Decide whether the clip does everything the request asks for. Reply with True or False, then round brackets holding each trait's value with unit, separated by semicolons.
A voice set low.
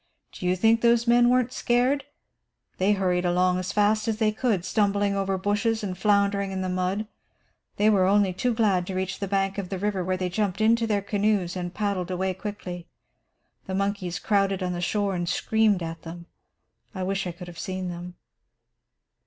False (195 Hz)